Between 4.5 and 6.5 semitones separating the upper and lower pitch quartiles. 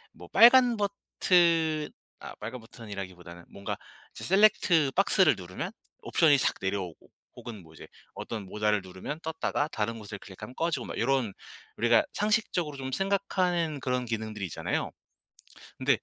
No: wide, 8.7 semitones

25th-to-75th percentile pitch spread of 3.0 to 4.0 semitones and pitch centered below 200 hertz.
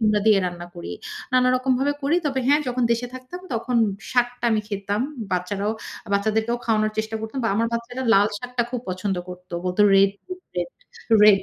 No: average, 3.7 semitones; high, 220 Hz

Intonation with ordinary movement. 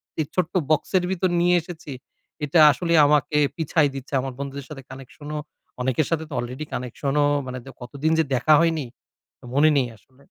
Yes: average, 3.2 semitones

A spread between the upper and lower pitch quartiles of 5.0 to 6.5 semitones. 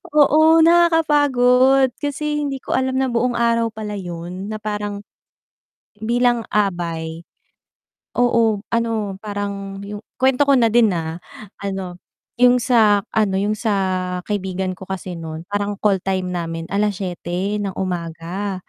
No: average, 4.5 semitones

